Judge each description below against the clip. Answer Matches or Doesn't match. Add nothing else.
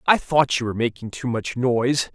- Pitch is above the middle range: Doesn't match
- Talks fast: Matches